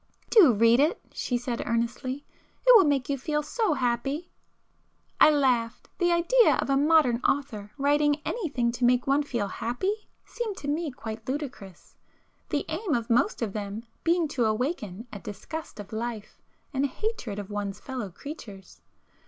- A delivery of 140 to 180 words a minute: Yes, average, 160 wpm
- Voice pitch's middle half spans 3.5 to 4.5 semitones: No, average, 5.0 semitones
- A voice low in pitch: No, very high, 260 Hz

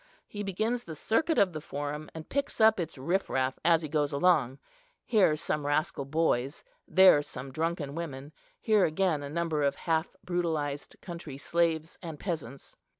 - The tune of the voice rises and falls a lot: No, average, 3.8 semitones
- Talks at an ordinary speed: Yes, average, 160 wpm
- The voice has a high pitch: No, medium, 160 Hz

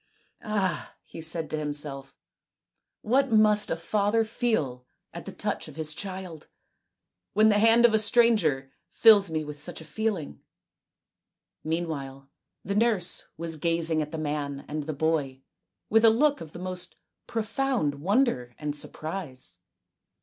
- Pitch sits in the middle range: Yes, medium, 165 Hz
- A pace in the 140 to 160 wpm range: Yes, average, 155 wpm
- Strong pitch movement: Yes, wide, 6.4 semitones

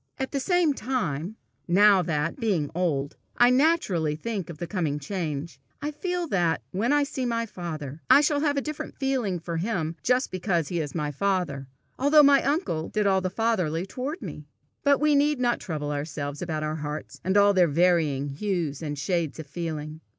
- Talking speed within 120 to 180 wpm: No, average, 190 wpm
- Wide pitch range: Yes, wide, 8.4 semitones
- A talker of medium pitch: Yes, medium, 180 Hz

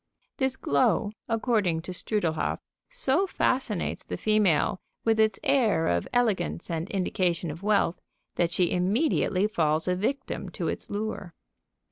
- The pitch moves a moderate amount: Yes, average, 4.7 semitones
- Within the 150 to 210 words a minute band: No, slow, 135 wpm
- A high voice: Yes, high, 200 Hz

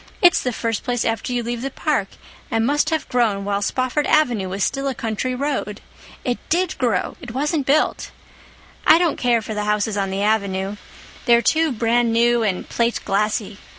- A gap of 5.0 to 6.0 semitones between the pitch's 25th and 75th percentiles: No, average, 4.2 semitones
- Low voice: No, high, 235 Hz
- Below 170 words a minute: No, average, 180 wpm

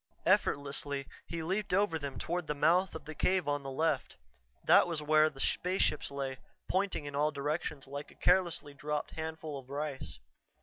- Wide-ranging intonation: No, average, 2.9 semitones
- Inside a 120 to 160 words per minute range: No, average, 175 wpm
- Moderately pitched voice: Yes, medium, 150 Hz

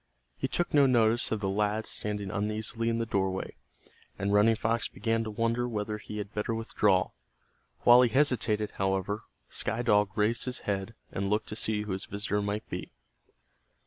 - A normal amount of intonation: No, narrow, 1.9 semitones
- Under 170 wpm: No, average, 175 wpm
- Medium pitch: No, low, 105 Hz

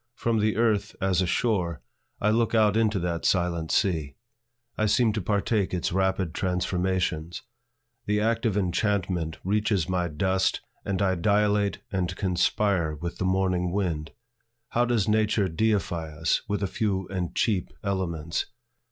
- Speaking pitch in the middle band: No, very low, 95 Hz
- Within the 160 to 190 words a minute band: No, average, 145 wpm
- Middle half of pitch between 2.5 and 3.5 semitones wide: Yes, average, 3.1 semitones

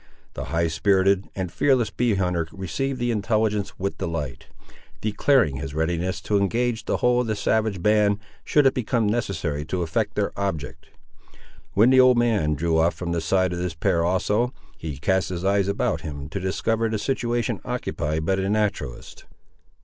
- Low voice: Yes, low, 100 Hz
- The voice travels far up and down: No, average, 5.0 semitones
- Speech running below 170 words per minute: No, average, 175 wpm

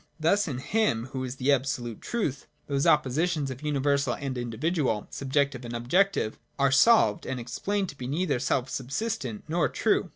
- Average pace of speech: Yes, average, 160 wpm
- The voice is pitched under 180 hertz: Yes, medium, 140 Hz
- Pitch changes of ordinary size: Yes, average, 4.2 semitones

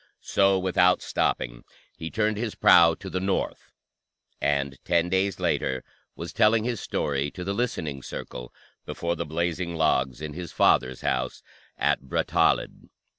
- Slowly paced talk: No, average, 145 wpm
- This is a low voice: Yes, very low, 85 Hz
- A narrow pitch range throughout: No, average, 5.3 semitones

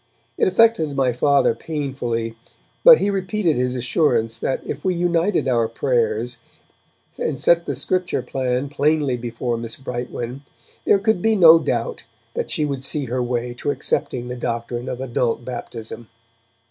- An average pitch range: No, wide, 5.9 semitones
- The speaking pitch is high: No, low, 135 Hz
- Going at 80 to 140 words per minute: No, average, 155 wpm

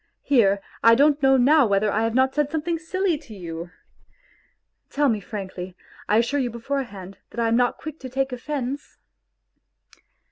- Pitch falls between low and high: No, very high, 250 Hz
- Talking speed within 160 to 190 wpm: Yes, average, 170 wpm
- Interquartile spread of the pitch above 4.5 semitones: Yes, average, 5.2 semitones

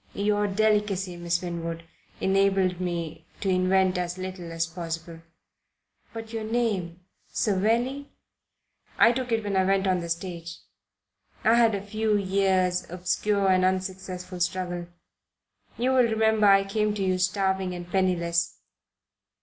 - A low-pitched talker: No, high, 190 Hz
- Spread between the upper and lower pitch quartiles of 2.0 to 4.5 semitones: Yes, average, 2.8 semitones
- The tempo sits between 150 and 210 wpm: No, slow, 135 wpm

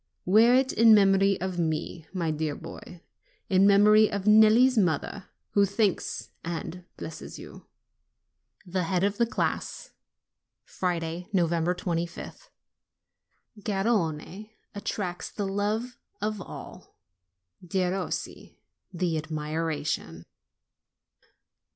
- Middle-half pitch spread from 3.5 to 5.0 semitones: Yes, average, 3.8 semitones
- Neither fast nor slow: No, slow, 100 wpm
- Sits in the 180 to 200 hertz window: Yes, high, 190 Hz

